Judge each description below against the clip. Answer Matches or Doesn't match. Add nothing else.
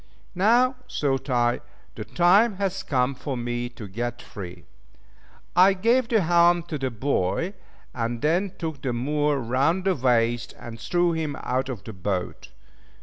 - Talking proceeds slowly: Doesn't match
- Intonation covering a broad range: Matches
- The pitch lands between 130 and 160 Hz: Matches